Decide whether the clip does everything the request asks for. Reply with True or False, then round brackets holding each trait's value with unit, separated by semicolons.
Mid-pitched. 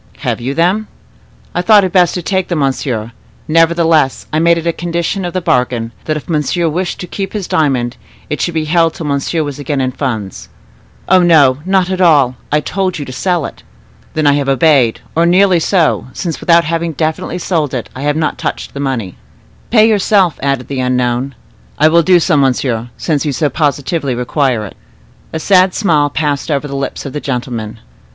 True (155 Hz)